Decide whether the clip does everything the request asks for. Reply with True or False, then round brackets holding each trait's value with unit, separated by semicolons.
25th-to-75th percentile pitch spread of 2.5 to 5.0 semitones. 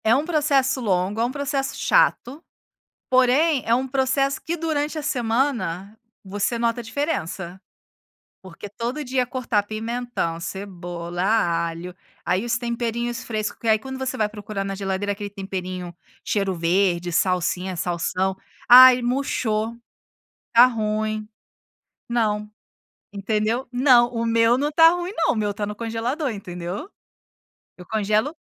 True (4.7 semitones)